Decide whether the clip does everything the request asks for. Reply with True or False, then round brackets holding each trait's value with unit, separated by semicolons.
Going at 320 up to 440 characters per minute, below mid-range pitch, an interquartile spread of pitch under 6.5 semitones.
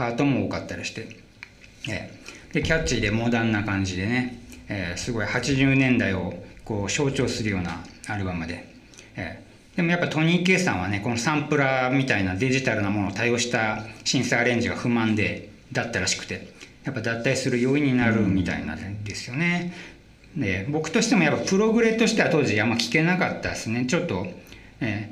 True (375 characters per minute; 120 Hz; 5.1 semitones)